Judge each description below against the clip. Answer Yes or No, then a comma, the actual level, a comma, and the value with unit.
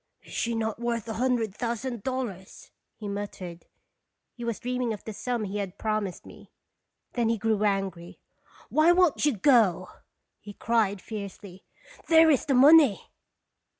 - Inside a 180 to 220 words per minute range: No, average, 165 wpm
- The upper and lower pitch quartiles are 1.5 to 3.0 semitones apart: No, average, 3.8 semitones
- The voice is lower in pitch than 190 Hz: No, high, 225 Hz